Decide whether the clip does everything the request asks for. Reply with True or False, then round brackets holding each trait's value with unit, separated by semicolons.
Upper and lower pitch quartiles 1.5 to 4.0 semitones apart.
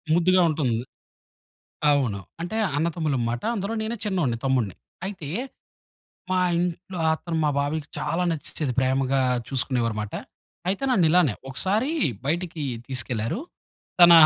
False (5.5 semitones)